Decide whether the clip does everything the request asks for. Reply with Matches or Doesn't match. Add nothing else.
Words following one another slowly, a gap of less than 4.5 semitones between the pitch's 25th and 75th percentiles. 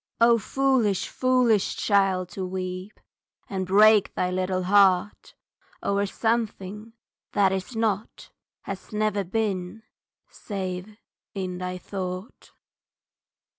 Matches